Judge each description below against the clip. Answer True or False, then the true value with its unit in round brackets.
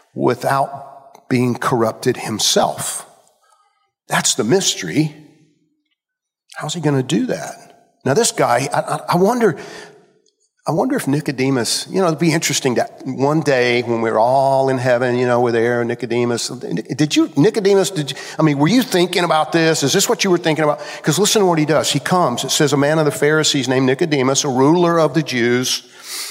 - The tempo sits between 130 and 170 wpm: False (190 wpm)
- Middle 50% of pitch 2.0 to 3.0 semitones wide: False (4.9 semitones)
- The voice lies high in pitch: False (150 Hz)